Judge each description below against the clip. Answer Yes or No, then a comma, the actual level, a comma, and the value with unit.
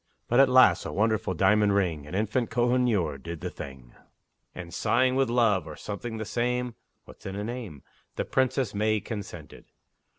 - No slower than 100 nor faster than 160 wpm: No, average, 170 wpm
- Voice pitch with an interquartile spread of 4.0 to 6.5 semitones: Yes, average, 4.9 semitones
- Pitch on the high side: No, low, 105 Hz